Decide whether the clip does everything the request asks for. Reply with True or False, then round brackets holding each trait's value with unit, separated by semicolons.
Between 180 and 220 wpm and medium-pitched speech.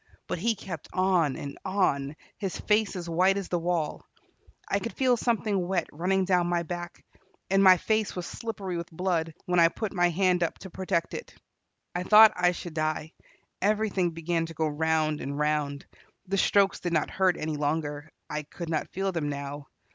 True (190 wpm; 175 Hz)